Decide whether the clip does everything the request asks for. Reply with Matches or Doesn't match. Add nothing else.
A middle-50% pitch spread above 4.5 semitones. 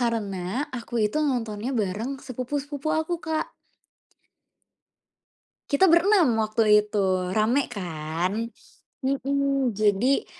Matches